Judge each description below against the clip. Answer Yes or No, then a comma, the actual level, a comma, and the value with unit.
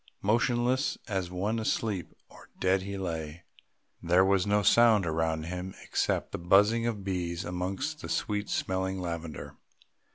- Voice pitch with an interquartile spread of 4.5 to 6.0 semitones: No, average, 3.2 semitones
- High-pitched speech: No, very low, 95 Hz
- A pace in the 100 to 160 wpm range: Yes, average, 140 wpm